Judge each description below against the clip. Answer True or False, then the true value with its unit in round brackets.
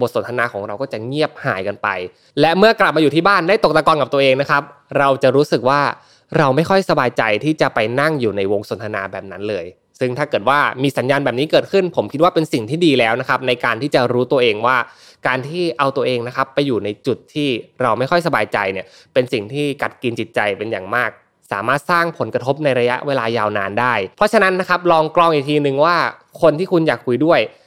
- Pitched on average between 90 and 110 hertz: False (140 Hz)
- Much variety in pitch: False (4.8 semitones)